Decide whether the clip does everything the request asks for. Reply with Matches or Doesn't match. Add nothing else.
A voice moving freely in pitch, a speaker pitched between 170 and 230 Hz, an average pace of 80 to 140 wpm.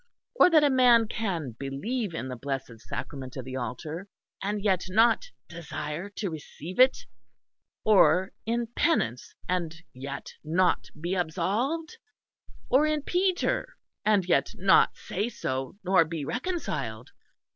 Matches